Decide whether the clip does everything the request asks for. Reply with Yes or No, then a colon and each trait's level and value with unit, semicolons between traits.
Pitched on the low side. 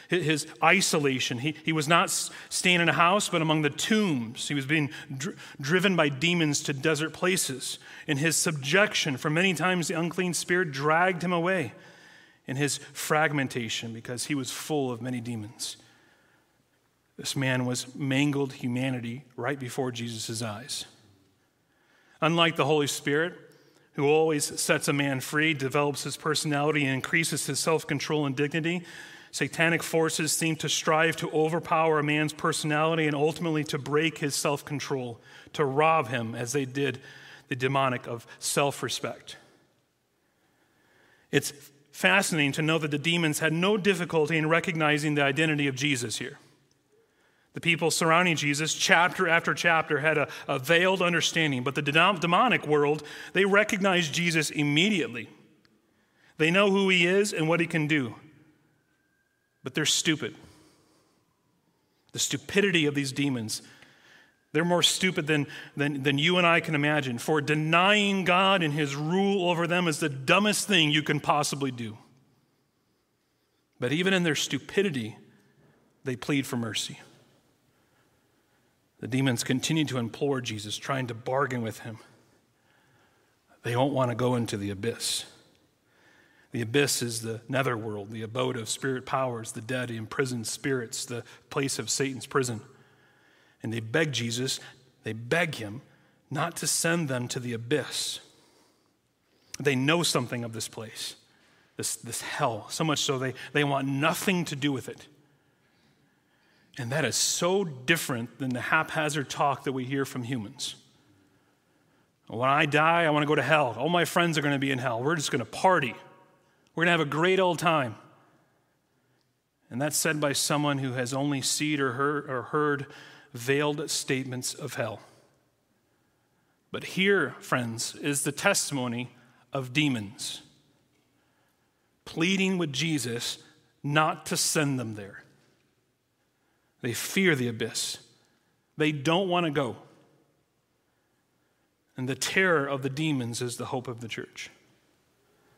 No: medium, 150 Hz